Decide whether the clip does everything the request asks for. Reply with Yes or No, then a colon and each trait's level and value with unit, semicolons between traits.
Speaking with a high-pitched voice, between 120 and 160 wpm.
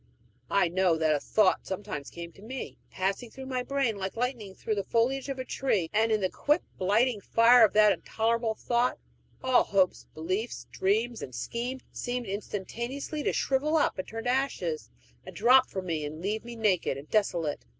No: high, 220 Hz; average, 190 wpm